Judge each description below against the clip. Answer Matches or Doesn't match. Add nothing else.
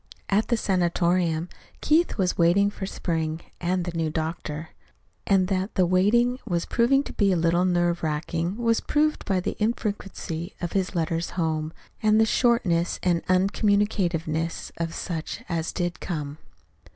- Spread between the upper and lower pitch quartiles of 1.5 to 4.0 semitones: Matches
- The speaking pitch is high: Doesn't match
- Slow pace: Doesn't match